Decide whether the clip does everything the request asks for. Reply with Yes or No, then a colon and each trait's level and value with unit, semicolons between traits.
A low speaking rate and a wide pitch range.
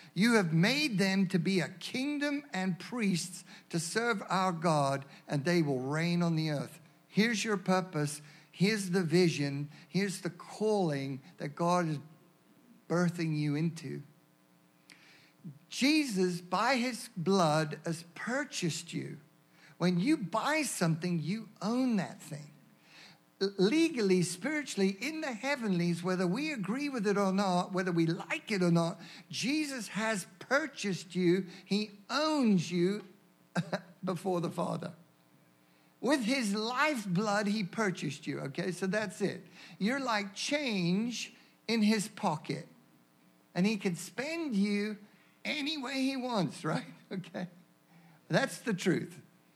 No: slow, 130 wpm; average, 4.4 semitones